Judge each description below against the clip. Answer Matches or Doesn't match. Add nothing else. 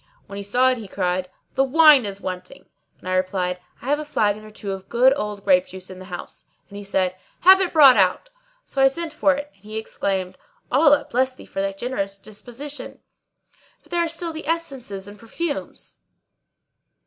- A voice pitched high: Matches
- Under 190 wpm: Doesn't match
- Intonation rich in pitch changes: Matches